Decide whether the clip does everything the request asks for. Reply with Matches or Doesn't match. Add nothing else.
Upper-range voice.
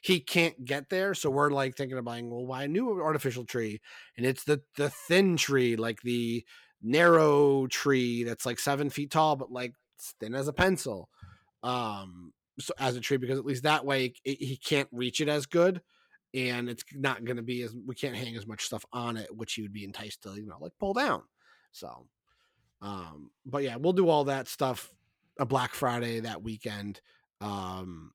Doesn't match